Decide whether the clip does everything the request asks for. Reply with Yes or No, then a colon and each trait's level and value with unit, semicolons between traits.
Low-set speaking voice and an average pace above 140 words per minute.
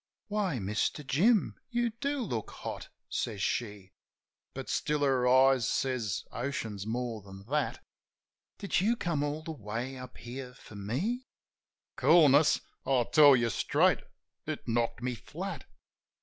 No: low, 130 Hz; slow, 135 wpm